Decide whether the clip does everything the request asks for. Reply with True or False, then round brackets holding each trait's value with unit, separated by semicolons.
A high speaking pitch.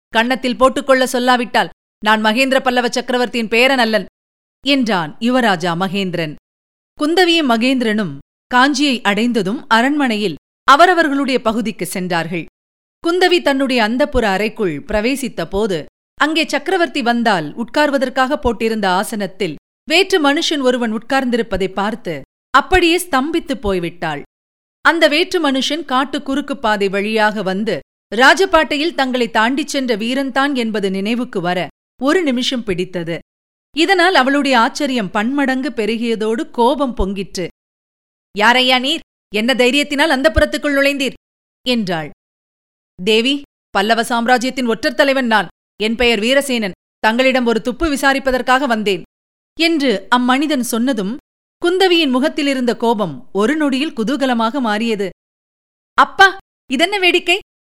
True (245 Hz)